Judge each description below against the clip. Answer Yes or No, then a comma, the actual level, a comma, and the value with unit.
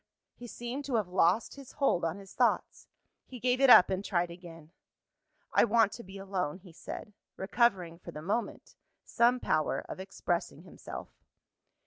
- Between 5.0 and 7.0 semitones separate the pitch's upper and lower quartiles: Yes, average, 5.3 semitones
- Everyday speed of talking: Yes, average, 165 wpm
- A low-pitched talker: No, high, 195 Hz